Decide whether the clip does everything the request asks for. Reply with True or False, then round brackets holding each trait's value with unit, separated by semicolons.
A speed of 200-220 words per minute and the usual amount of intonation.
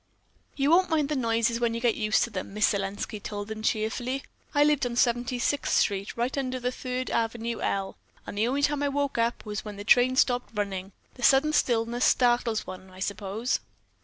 True (205 wpm; 3.4 semitones)